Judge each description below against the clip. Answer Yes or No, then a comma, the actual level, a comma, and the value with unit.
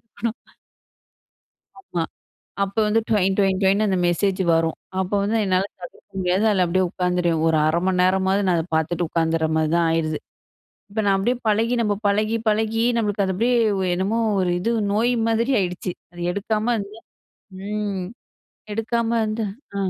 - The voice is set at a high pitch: Yes, high, 195 Hz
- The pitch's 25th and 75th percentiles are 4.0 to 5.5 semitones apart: No, average, 3.3 semitones